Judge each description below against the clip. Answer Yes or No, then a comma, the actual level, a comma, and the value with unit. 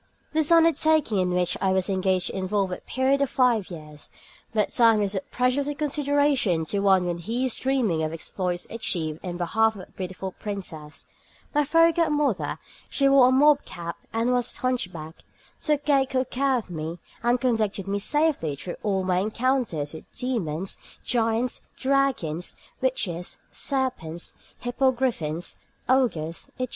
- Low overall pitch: No, high, 220 Hz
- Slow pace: No, average, 155 wpm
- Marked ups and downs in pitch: Yes, wide, 6.7 semitones